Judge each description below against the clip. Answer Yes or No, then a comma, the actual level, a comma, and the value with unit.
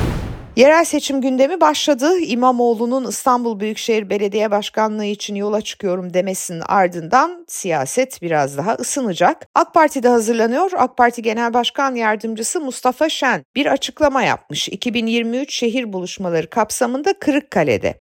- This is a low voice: No, high, 235 Hz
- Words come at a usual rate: Yes, average, 125 wpm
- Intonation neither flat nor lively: Yes, average, 4.4 semitones